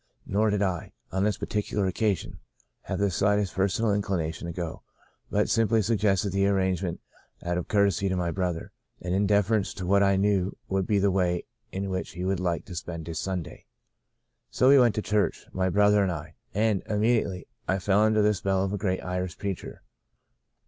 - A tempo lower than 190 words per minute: No, average, 195 wpm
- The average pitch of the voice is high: No, very low, 95 Hz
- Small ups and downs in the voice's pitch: Yes, narrow, 2.2 semitones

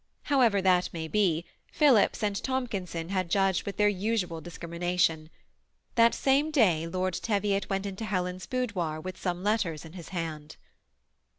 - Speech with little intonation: No, average, 3.7 semitones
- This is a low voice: No, medium, 185 Hz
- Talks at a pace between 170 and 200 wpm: No, average, 155 wpm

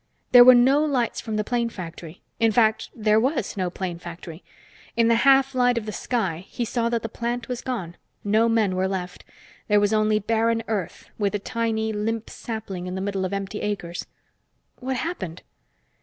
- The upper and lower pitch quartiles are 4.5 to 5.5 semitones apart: No, average, 3.5 semitones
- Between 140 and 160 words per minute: No, average, 190 wpm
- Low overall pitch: No, high, 220 Hz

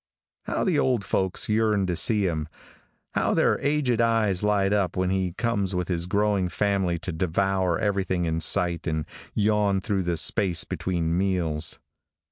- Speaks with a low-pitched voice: Yes, very low, 95 Hz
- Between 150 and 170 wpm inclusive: Yes, average, 160 wpm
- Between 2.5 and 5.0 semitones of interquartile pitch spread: Yes, average, 3.0 semitones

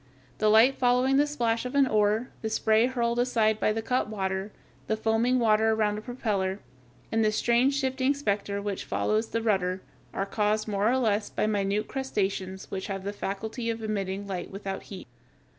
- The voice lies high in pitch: Yes, high, 215 Hz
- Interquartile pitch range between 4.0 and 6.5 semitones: No, average, 2.9 semitones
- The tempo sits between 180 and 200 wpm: Yes, average, 185 wpm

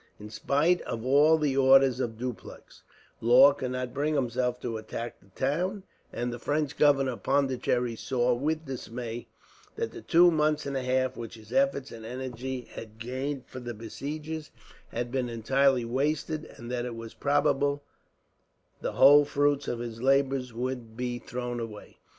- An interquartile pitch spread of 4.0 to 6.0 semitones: No, average, 3.0 semitones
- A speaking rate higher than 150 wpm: Yes, average, 170 wpm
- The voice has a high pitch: No, low, 130 Hz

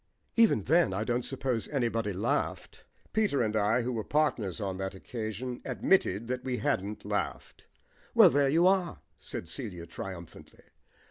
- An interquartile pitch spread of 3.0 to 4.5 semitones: No, wide, 5.4 semitones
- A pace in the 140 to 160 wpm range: Yes, average, 150 wpm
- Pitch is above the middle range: No, low, 120 Hz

